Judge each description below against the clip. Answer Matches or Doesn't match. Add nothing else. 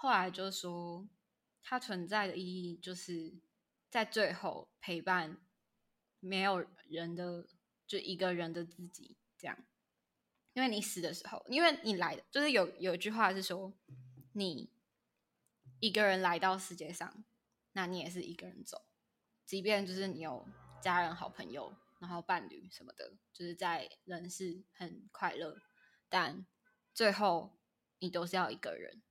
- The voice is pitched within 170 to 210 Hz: Matches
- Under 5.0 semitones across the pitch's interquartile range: Matches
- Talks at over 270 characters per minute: Doesn't match